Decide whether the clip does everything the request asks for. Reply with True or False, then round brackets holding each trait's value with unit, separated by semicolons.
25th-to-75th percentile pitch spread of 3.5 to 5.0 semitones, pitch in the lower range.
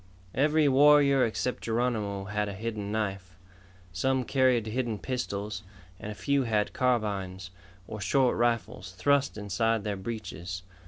True (4.2 semitones; 110 Hz)